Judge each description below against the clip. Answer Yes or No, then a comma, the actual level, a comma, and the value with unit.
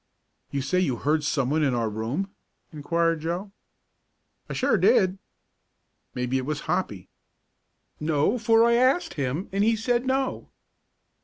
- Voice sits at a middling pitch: Yes, medium, 165 Hz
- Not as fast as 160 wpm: Yes, average, 140 wpm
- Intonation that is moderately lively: No, wide, 7.1 semitones